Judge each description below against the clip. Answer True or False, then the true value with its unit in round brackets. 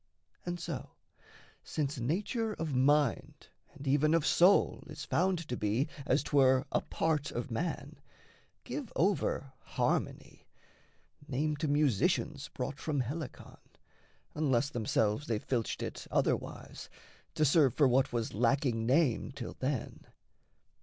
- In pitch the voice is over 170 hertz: False (140 Hz)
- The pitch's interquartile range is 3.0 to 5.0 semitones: True (3.6 semitones)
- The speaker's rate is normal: False (125 wpm)